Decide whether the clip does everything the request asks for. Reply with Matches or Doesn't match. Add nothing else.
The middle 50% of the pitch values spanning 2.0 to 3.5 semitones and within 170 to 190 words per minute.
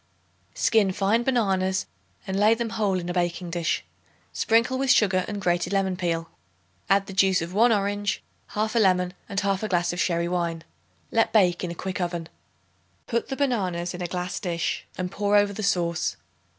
Matches